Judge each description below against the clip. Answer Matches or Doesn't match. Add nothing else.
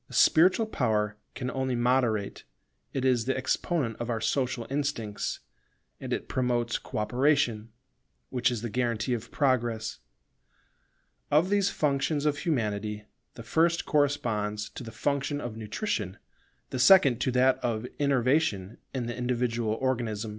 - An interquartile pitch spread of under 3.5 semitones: Doesn't match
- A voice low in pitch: Matches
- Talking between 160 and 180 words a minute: Doesn't match